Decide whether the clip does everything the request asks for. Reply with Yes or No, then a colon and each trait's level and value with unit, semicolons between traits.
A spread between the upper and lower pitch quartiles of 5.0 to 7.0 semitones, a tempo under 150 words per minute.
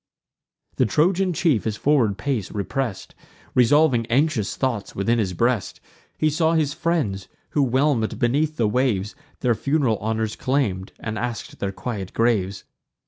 Yes: wide, 5.5 semitones; average, 140 wpm